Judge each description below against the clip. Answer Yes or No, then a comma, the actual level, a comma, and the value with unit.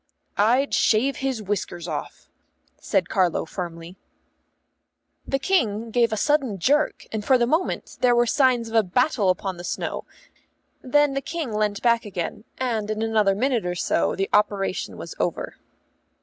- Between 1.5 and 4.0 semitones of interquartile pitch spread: No, average, 4.8 semitones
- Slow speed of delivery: No, average, 160 wpm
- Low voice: No, high, 220 Hz